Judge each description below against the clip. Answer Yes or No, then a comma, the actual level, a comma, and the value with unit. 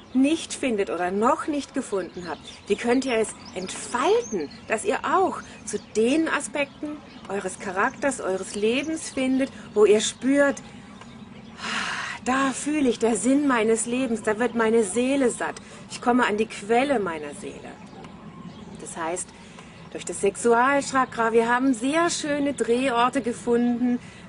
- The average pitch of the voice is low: No, high, 235 Hz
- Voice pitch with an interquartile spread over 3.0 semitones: Yes, average, 4.1 semitones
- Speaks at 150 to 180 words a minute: No, average, 140 wpm